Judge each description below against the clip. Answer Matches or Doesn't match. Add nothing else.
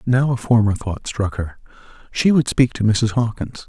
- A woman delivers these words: Doesn't match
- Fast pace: Doesn't match